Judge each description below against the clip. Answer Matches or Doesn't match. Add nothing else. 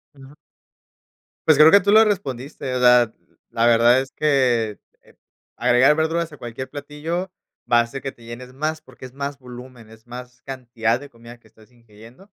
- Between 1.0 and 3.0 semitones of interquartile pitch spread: Doesn't match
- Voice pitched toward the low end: Matches